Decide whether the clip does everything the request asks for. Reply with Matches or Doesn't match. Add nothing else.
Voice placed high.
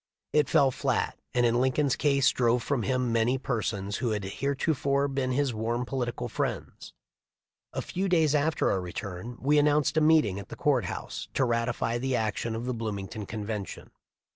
Doesn't match